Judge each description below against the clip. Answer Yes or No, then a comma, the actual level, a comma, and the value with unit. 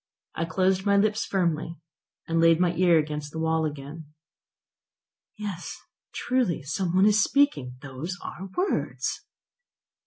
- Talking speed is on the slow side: Yes, slow, 130 wpm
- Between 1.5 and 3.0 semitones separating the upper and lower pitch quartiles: No, average, 3.8 semitones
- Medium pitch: Yes, medium, 170 Hz